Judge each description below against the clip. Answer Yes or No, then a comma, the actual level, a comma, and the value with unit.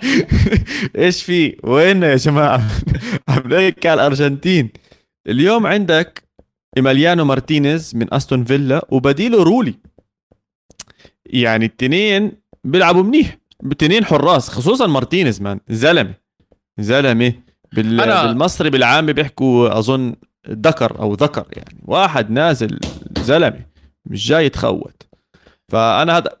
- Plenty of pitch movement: Yes, wide, 6.6 semitones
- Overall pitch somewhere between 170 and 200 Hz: No, medium, 140 Hz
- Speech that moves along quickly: No, average, 100 wpm